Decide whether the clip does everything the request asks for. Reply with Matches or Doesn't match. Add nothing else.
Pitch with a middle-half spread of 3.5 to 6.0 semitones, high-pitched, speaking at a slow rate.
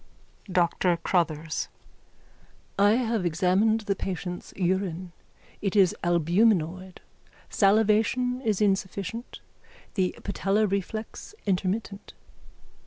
Doesn't match